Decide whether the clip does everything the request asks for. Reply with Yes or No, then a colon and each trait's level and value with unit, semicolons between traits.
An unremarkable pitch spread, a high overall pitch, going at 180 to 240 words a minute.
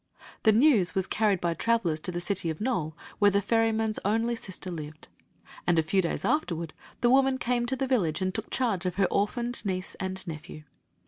Yes: average, 5.0 semitones; high, 200 Hz; average, 200 wpm